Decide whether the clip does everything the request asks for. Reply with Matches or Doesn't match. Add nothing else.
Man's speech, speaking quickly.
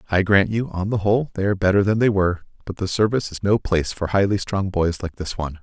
Matches